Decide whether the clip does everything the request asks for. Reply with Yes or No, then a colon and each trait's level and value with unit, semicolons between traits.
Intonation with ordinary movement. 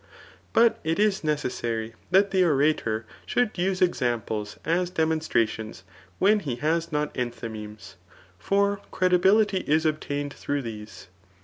No: wide, 8.0 semitones